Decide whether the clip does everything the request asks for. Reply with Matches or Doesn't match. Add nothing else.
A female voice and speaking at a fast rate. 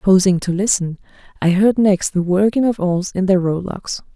Doesn't match